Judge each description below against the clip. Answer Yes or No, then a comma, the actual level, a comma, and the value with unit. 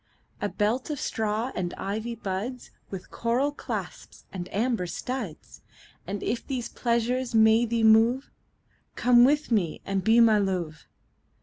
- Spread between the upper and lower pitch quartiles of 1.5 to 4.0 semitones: Yes, average, 3.6 semitones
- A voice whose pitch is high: Yes, high, 225 Hz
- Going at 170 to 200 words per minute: No, average, 145 wpm